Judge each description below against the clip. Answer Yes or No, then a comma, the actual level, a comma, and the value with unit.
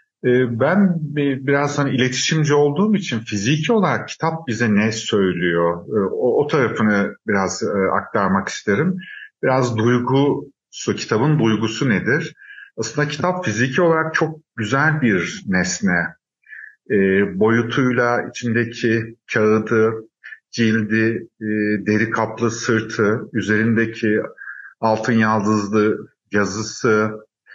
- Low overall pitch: Yes, low, 115 Hz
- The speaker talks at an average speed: No, slow, 90 wpm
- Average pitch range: Yes, average, 4.5 semitones